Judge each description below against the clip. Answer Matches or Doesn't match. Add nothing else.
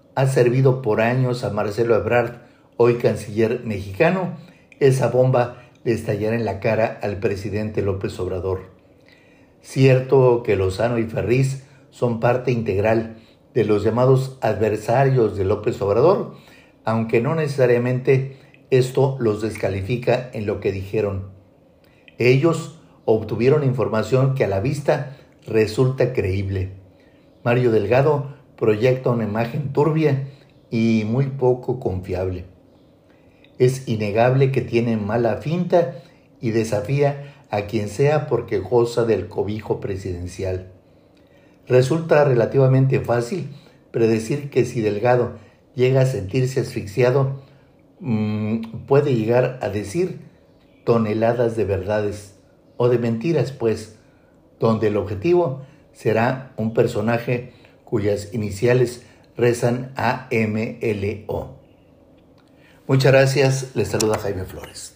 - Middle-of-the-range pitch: Doesn't match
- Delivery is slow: Matches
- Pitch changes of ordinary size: Matches